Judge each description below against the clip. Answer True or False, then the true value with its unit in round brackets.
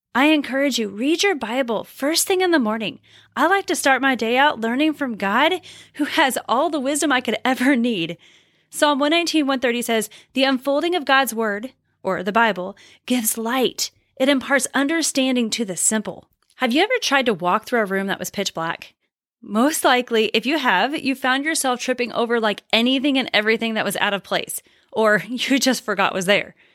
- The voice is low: False (255 Hz)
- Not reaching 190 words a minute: False (195 wpm)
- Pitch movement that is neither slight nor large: True (4.7 semitones)